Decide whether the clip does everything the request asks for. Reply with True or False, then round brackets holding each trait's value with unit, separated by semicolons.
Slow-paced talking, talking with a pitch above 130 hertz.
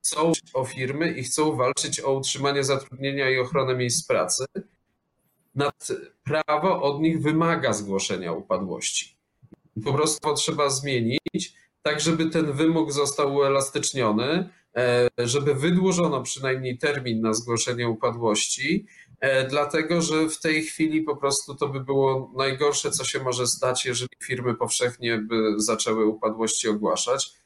False (130 wpm; 140 Hz)